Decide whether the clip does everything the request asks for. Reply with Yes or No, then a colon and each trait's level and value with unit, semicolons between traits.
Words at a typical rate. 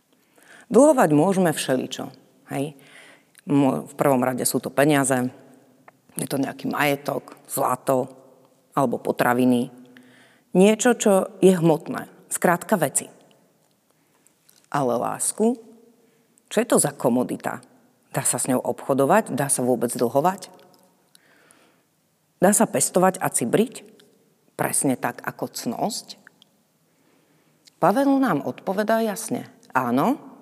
No: slow, 105 wpm